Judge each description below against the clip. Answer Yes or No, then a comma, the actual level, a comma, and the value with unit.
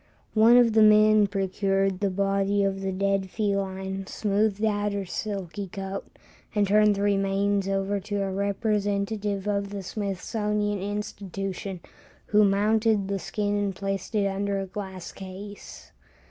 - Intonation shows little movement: Yes, narrow, 1.2 semitones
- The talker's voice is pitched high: Yes, high, 200 Hz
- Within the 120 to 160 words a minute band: Yes, average, 145 wpm